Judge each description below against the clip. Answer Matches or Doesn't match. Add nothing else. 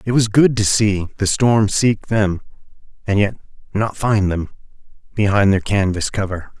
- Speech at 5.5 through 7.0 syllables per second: Doesn't match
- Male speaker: Matches